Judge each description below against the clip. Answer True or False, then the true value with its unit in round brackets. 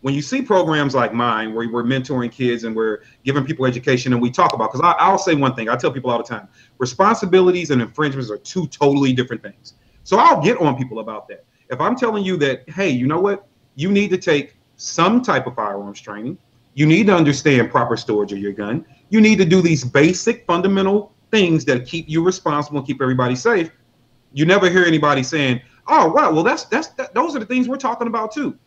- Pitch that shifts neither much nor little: False (7.0 semitones)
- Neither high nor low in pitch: True (145 Hz)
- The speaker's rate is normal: False (225 wpm)